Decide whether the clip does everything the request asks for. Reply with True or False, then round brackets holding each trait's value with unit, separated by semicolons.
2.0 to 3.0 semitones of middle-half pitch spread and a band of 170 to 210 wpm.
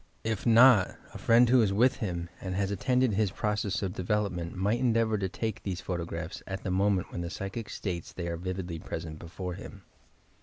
False (3.6 semitones; 200 wpm)